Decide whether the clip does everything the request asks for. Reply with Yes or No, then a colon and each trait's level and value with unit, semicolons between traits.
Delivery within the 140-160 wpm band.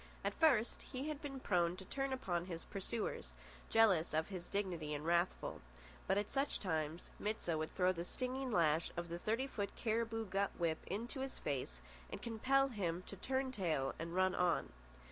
No: average, 185 wpm